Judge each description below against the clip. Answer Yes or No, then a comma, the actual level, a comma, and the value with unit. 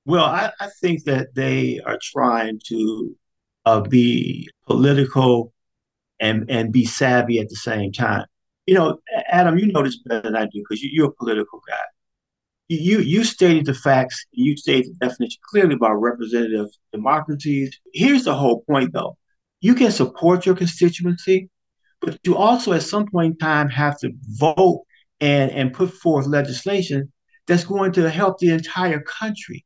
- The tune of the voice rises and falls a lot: Yes, wide, 7.3 semitones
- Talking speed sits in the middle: Yes, average, 165 wpm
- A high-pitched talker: No, medium, 145 Hz